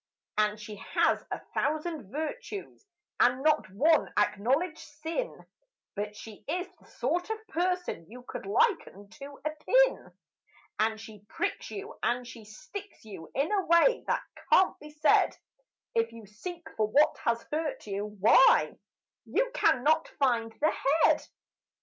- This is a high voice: Yes, very high, 295 Hz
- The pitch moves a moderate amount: No, wide, 8.5 semitones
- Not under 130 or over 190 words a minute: Yes, average, 145 wpm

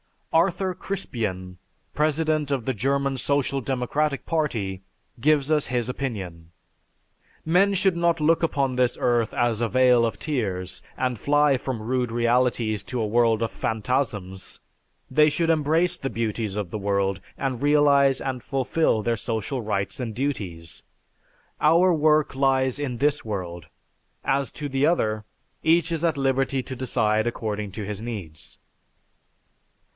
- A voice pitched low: Yes, low, 130 Hz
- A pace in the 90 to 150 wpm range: Yes, average, 145 wpm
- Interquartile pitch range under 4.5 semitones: No, average, 5.1 semitones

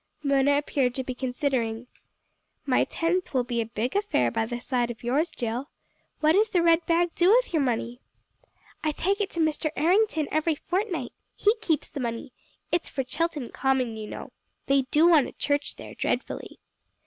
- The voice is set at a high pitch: Yes, very high, 285 Hz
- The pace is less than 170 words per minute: No, average, 185 wpm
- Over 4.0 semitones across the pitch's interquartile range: Yes, average, 5.3 semitones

